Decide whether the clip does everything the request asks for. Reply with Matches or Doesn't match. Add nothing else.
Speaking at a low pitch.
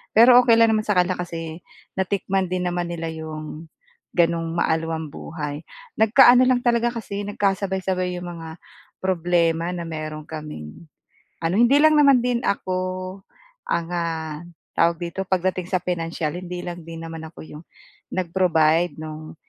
Doesn't match